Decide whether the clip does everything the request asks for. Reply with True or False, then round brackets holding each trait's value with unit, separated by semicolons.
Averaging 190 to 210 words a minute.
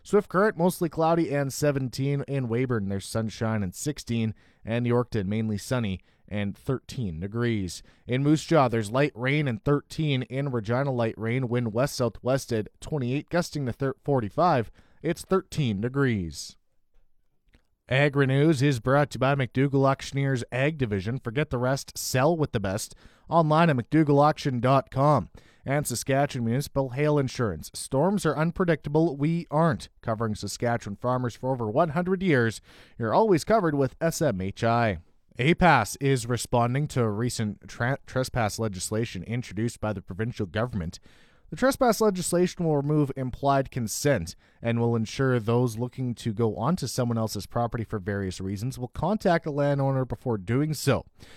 False (150 wpm)